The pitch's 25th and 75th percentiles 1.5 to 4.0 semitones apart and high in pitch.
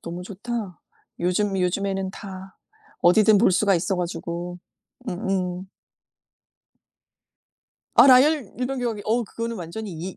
Yes: average, 3.5 semitones; high, 195 Hz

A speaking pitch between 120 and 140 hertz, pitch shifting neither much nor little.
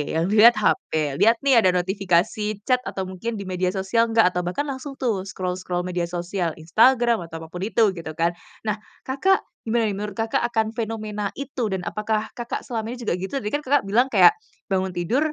No: high, 210 Hz; average, 4.4 semitones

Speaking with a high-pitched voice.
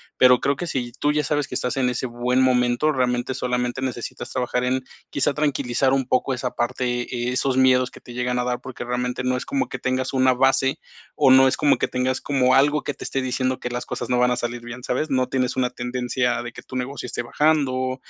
No: low, 125 Hz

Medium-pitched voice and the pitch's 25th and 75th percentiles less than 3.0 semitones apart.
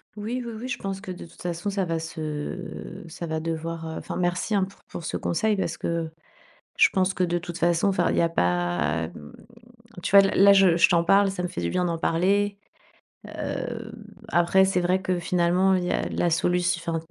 Yes: medium, 175 Hz; narrow, 2.6 semitones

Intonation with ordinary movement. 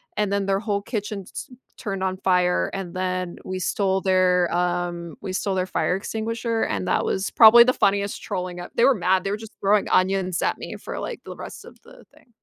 No: narrow, 2.1 semitones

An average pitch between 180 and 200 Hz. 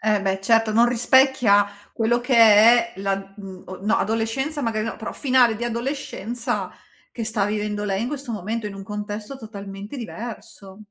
No: high, 220 Hz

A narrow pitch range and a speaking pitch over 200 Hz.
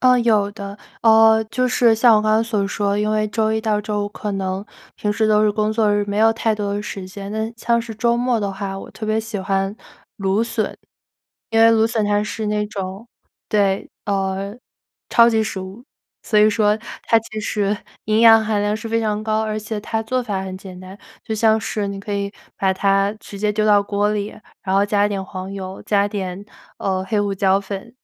Yes: narrow, 1.8 semitones; high, 210 Hz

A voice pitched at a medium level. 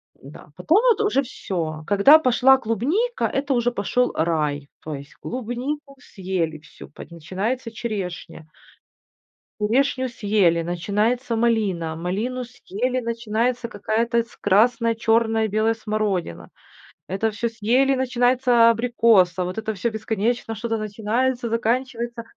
No: high, 225 Hz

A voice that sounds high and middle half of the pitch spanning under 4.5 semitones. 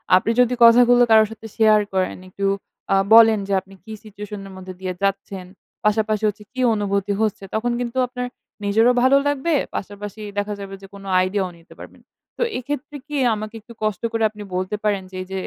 Yes: high, 210 Hz; average, 2.7 semitones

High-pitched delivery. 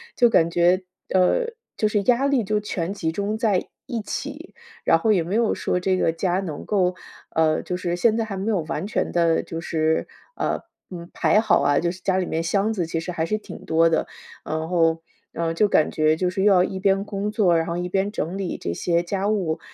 No: medium, 180 Hz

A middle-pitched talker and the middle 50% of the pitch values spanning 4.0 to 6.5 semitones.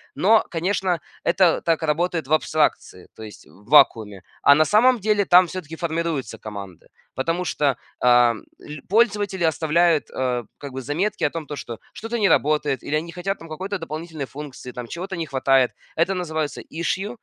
Yes: medium, 160 Hz; average, 5.1 semitones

